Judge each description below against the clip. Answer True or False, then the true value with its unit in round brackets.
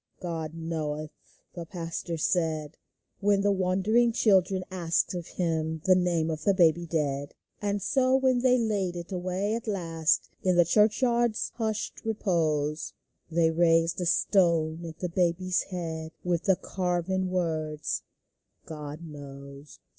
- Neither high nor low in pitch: True (175 Hz)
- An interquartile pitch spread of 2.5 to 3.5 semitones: True (3.2 semitones)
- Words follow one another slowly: False (145 wpm)